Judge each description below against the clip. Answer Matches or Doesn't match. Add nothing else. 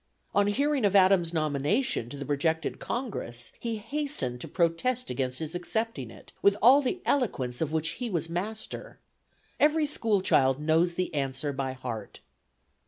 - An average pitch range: Doesn't match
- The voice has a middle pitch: Matches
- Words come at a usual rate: Matches